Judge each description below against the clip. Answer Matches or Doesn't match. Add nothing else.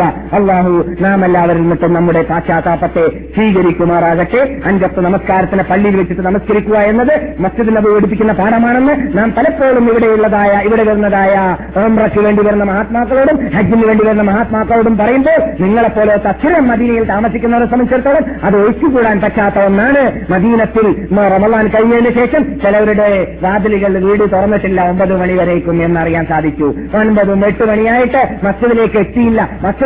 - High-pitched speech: Matches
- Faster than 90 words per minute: Matches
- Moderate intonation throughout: Matches